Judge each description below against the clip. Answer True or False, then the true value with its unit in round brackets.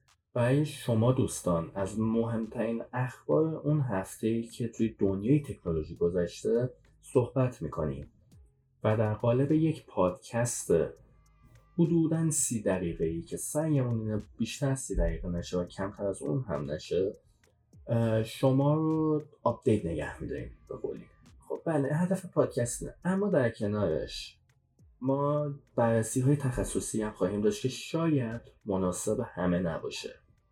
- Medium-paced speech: True (120 wpm)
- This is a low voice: True (115 Hz)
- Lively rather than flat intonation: True (6.4 semitones)